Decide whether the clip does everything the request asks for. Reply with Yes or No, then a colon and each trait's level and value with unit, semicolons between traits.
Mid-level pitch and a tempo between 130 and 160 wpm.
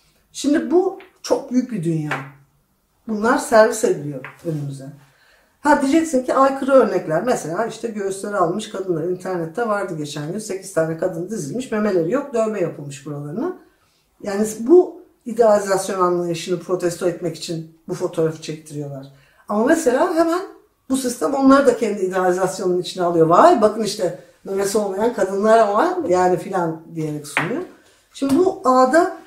No: high, 195 Hz; fast, 140 wpm